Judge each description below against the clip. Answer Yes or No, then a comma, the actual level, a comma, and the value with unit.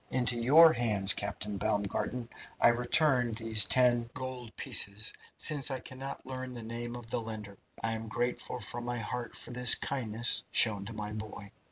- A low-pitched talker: Yes, low, 120 Hz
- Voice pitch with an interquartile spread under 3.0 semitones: Yes, narrow, 2.5 semitones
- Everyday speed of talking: Yes, average, 170 wpm